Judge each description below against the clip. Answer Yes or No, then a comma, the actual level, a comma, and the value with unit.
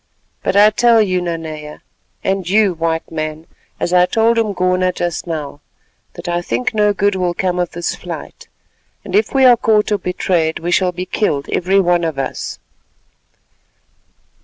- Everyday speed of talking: Yes, average, 165 wpm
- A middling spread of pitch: Yes, average, 3.6 semitones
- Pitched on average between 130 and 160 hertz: No, medium, 180 Hz